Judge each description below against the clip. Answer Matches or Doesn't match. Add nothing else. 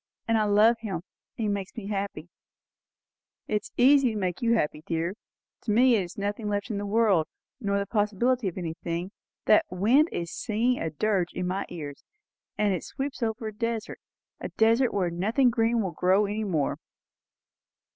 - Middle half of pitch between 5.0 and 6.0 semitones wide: Doesn't match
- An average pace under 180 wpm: Doesn't match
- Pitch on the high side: Matches